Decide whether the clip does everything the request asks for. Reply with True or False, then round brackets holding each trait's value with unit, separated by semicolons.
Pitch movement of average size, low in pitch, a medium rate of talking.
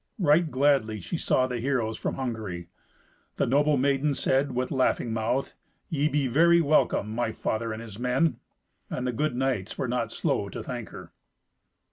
True (3.9 semitones; 130 Hz; 170 wpm)